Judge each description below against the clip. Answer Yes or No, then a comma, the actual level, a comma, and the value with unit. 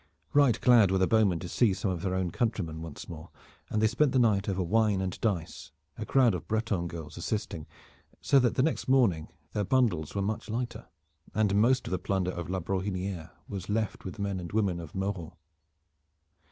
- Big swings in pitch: No, average, 4.0 semitones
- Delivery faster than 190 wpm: Yes, average, 200 wpm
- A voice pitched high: No, low, 100 Hz